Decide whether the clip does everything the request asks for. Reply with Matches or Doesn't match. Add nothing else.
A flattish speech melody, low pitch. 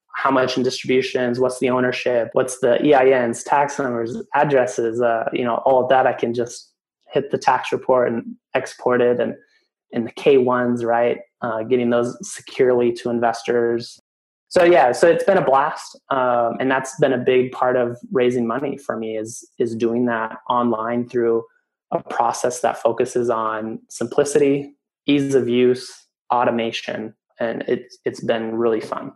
Matches